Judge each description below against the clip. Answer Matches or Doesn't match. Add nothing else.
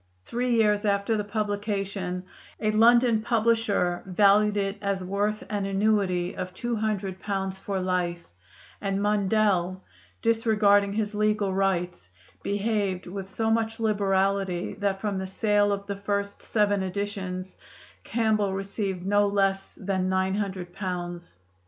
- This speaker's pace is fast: Doesn't match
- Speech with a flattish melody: Matches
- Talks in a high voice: Matches